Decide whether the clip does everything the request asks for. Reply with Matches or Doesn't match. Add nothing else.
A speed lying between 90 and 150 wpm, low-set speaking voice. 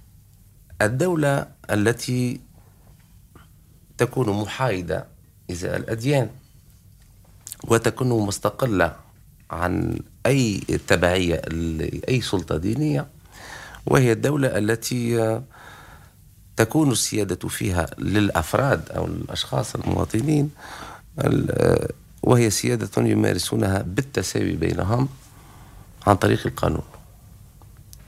Doesn't match